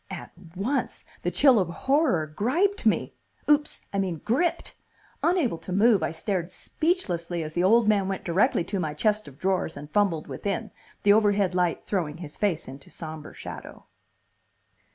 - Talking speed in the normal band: Yes, average, 165 wpm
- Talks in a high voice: Yes, high, 195 Hz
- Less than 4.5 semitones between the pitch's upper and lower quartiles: No, average, 5.0 semitones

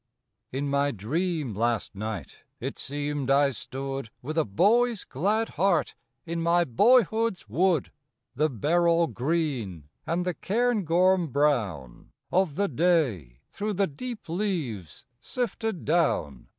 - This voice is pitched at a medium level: Yes, medium, 155 Hz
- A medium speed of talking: No, slow, 125 wpm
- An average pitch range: No, wide, 6.7 semitones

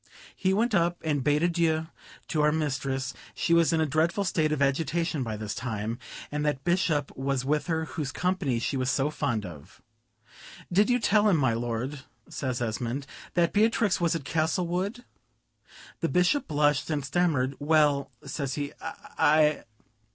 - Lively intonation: No, average, 4.2 semitones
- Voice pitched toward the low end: No, medium, 150 Hz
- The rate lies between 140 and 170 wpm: Yes, average, 165 wpm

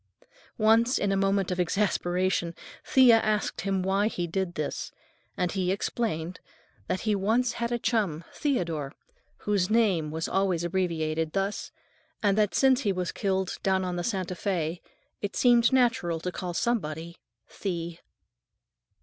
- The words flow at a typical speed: Yes, average, 150 wpm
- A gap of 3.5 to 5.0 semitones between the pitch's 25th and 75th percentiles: Yes, average, 3.8 semitones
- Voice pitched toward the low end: No, high, 190 Hz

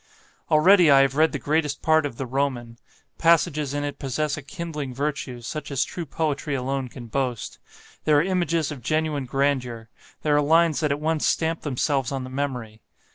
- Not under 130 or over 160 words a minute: No, average, 185 wpm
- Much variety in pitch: No, average, 2.9 semitones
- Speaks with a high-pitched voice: No, medium, 145 Hz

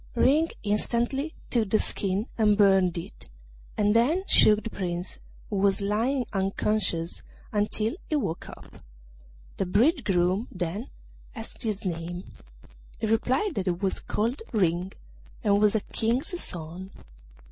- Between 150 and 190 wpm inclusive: No, slow, 135 wpm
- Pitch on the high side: Yes, high, 210 Hz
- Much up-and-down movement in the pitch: No, average, 3.7 semitones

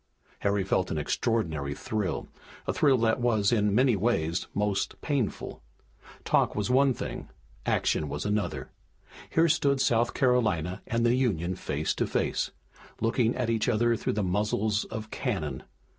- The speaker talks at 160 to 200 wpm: No, average, 150 wpm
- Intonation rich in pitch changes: No, average, 4.4 semitones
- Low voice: Yes, low, 110 Hz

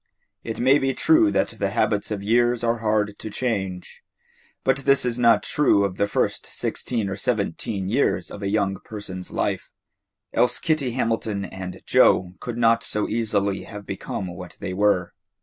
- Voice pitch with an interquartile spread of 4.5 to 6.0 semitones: No, average, 3.4 semitones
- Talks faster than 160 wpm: Yes, average, 170 wpm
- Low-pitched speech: Yes, low, 105 Hz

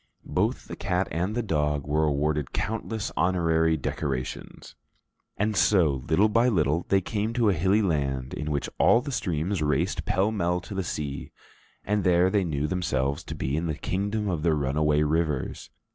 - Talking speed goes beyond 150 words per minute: Yes, average, 175 wpm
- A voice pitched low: Yes, very low, 85 Hz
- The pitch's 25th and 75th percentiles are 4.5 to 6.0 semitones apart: Yes, average, 5.0 semitones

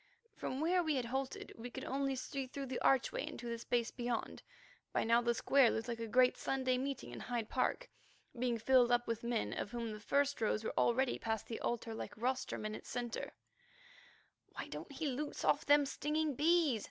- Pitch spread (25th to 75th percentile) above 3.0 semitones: No, average, 2.7 semitones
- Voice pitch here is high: Yes, very high, 250 Hz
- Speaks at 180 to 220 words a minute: Yes, average, 200 wpm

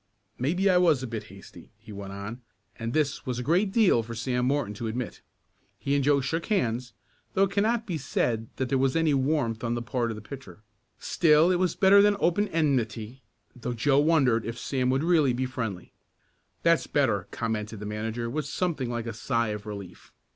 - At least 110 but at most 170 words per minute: No, fast, 205 wpm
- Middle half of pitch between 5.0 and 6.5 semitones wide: Yes, wide, 5.5 semitones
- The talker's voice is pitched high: No, low, 130 Hz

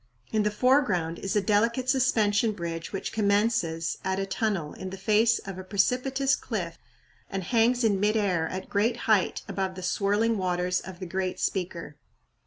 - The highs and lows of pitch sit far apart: No, average, 3.5 semitones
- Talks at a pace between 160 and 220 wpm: Yes, average, 175 wpm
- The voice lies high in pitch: Yes, high, 200 Hz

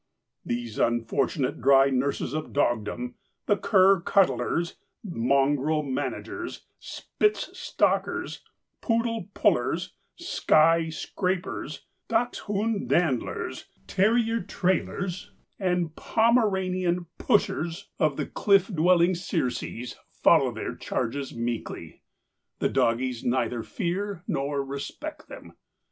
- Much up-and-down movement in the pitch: Yes, wide, 6.7 semitones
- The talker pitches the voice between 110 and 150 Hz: No, medium, 170 Hz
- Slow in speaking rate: Yes, slow, 95 wpm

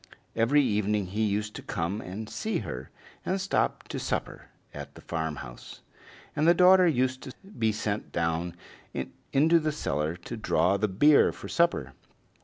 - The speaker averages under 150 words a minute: No, average, 160 wpm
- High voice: No, low, 110 Hz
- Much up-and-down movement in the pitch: Yes, wide, 8.8 semitones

